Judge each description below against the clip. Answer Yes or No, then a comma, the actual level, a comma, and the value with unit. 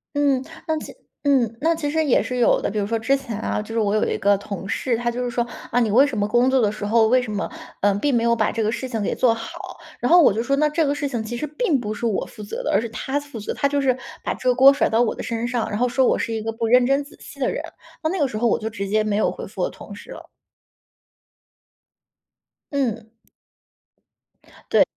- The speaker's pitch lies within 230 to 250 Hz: Yes, high, 235 Hz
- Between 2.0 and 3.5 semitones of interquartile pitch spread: No, average, 3.9 semitones